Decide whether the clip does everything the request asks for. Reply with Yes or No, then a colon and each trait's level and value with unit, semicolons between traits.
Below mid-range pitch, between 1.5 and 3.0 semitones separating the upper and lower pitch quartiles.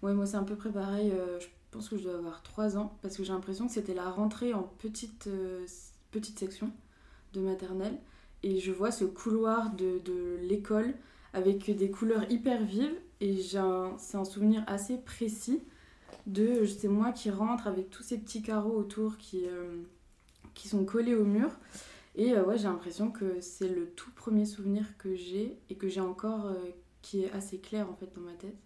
No: high, 205 Hz; narrow, 2.6 semitones